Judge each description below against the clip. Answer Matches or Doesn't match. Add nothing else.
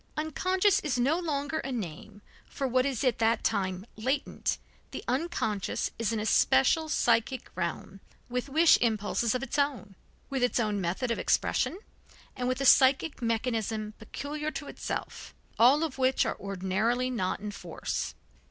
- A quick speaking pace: Doesn't match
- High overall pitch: Matches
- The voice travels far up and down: Doesn't match